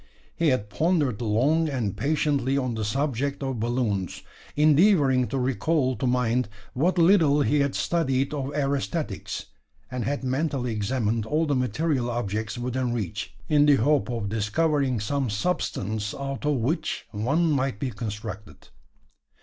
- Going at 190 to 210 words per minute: No, average, 145 wpm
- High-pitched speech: No, low, 130 Hz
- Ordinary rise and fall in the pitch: Yes, average, 4.3 semitones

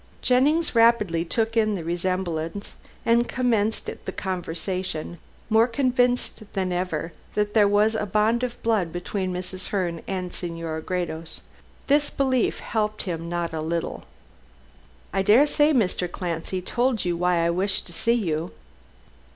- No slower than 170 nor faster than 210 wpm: No, average, 145 wpm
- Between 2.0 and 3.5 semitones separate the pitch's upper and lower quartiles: No, average, 4.8 semitones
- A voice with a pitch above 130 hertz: Yes, high, 190 Hz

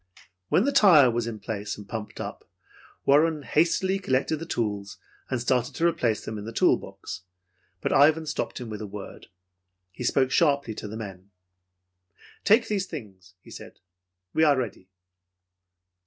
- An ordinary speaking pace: Yes, average, 165 wpm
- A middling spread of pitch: No, wide, 7.0 semitones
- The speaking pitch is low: Yes, low, 125 Hz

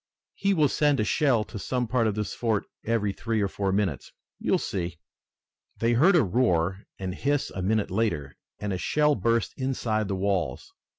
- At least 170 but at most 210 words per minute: Yes, average, 190 wpm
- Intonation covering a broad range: No, average, 4.5 semitones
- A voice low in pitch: Yes, low, 110 Hz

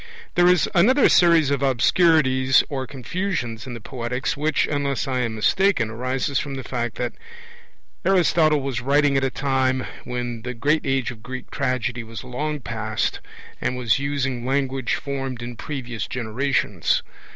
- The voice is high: No, low, 130 Hz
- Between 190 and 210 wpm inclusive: No, average, 155 wpm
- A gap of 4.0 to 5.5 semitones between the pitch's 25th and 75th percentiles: No, average, 2.9 semitones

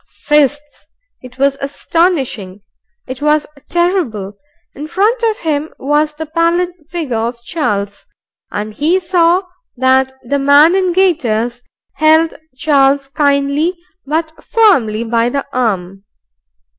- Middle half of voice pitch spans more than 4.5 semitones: Yes, average, 5.2 semitones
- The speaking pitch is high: Yes, very high, 290 Hz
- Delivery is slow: Yes, slow, 120 wpm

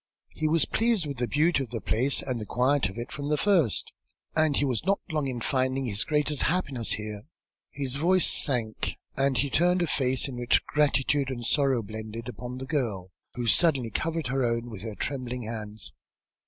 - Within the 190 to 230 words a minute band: Yes, average, 195 wpm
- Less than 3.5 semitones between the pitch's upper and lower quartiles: No, average, 4.1 semitones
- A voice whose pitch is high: No, low, 130 Hz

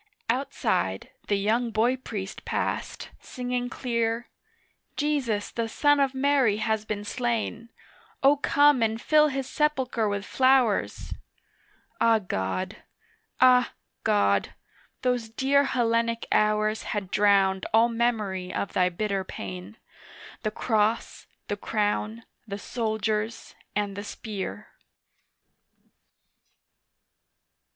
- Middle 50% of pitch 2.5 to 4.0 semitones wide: Yes, average, 3.3 semitones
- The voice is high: Yes, high, 225 Hz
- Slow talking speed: Yes, slow, 105 wpm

